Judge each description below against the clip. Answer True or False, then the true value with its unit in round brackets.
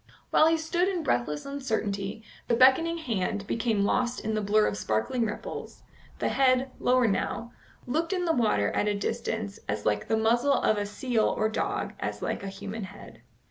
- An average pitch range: True (4.4 semitones)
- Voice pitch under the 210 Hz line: False (225 Hz)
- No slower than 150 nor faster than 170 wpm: False (185 wpm)